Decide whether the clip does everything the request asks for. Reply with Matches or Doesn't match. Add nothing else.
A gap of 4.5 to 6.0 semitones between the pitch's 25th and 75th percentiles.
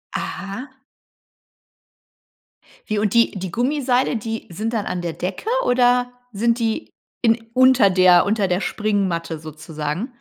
Matches